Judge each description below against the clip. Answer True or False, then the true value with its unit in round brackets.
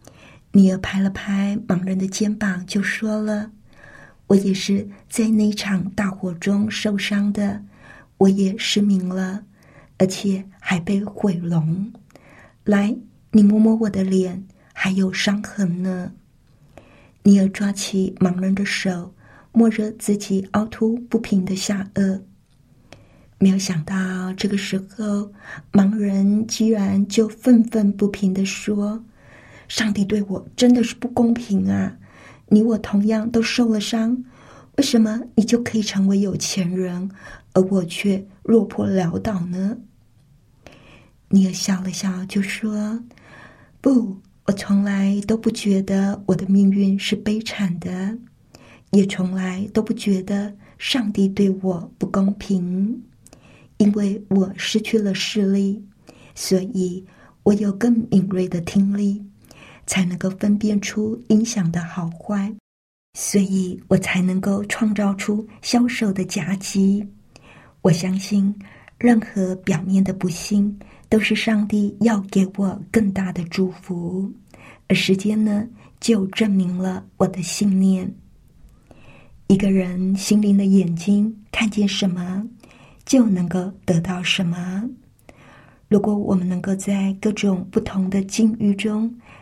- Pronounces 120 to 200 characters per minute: True (185 characters per minute)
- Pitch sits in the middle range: False (200 Hz)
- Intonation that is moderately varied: False (1.9 semitones)